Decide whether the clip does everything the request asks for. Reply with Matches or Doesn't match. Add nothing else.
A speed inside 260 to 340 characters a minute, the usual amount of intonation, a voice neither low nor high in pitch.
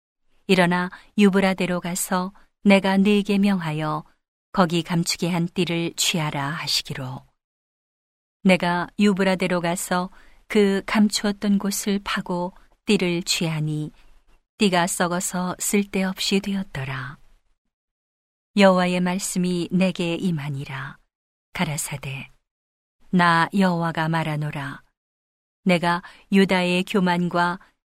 Doesn't match